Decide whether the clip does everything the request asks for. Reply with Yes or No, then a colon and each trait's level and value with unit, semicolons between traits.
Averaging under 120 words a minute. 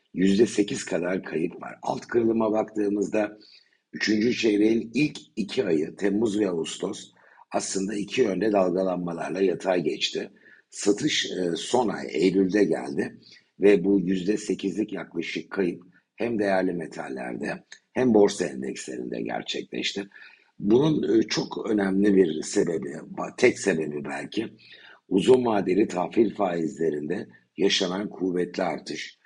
Yes: average, 110 wpm